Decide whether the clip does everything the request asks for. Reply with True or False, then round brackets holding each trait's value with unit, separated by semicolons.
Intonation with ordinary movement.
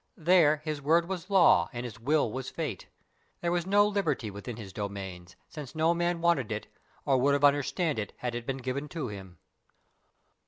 False (6.8 semitones)